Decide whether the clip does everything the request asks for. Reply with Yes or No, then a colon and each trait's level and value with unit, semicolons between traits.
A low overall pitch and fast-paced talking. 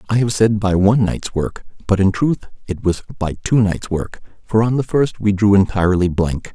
Yes: low, 100 Hz; fast, 220 wpm